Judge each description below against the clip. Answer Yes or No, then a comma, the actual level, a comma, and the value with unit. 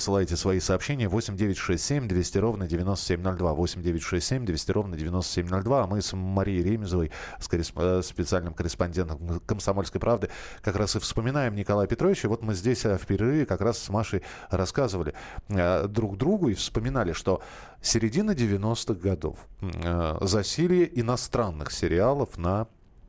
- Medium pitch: No, low, 100 Hz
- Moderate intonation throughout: Yes, average, 4.1 semitones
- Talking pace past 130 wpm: No, average, 125 wpm